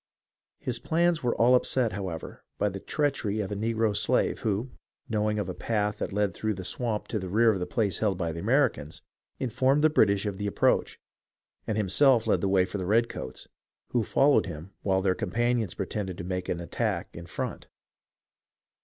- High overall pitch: No, low, 105 Hz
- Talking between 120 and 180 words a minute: No, average, 190 wpm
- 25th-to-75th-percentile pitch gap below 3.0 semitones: No, average, 3.8 semitones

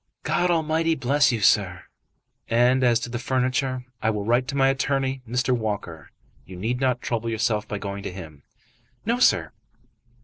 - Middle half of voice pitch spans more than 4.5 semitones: No, average, 4.1 semitones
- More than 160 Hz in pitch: No, low, 125 Hz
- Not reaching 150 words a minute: No, average, 170 wpm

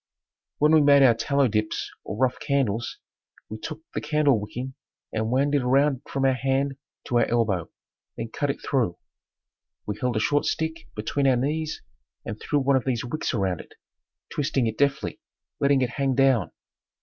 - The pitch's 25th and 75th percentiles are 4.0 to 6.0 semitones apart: No, average, 3.6 semitones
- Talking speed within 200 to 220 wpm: No, average, 175 wpm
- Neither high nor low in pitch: No, low, 130 Hz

